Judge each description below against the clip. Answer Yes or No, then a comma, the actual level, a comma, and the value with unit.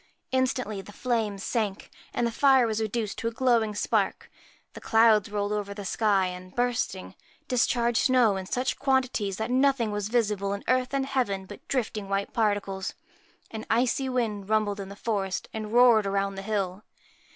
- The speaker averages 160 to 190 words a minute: Yes, average, 175 wpm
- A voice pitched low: No, high, 220 Hz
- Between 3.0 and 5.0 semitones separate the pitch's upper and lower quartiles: Yes, average, 3.4 semitones